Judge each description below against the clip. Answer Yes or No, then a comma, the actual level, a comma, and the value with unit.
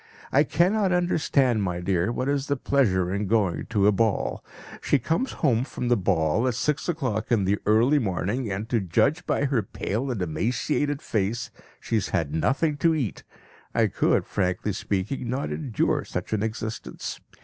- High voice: No, low, 115 Hz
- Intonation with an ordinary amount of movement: No, wide, 6.1 semitones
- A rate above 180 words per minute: No, average, 175 wpm